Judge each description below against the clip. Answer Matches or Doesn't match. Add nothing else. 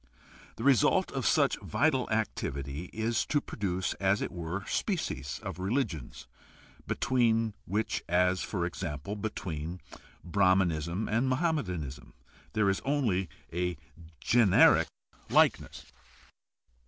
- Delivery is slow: Matches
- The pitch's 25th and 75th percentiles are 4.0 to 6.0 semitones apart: Matches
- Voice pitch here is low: Matches